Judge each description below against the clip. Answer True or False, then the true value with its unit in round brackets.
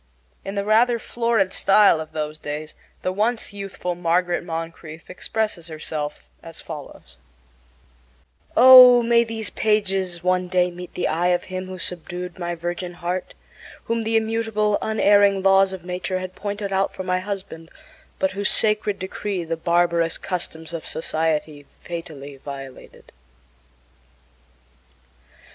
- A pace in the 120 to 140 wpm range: True (135 wpm)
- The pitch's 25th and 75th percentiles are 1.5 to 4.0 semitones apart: True (3.6 semitones)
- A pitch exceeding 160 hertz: True (185 Hz)